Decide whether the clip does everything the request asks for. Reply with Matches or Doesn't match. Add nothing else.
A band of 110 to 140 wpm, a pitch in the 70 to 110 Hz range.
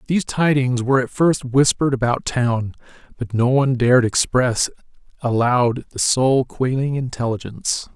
Doesn't match